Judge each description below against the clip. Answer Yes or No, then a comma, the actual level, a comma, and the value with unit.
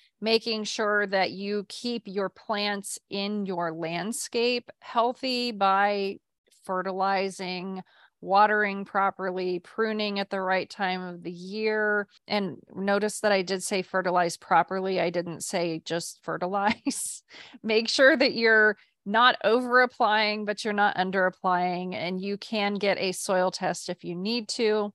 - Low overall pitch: No, high, 200 Hz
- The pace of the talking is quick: No, average, 140 wpm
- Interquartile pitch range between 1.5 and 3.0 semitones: Yes, average, 2.7 semitones